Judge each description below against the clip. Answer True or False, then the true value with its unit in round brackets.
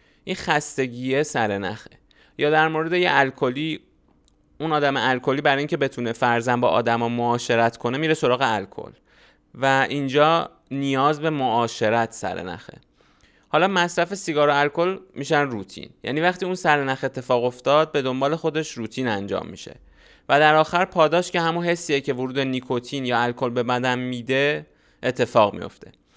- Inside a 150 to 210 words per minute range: True (155 wpm)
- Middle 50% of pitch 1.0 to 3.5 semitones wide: False (4.3 semitones)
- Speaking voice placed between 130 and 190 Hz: True (135 Hz)